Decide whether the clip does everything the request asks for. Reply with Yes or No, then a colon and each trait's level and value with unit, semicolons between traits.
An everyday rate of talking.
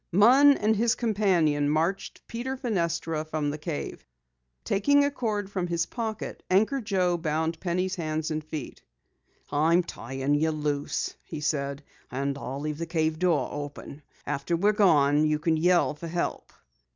Yes: average, 155 wpm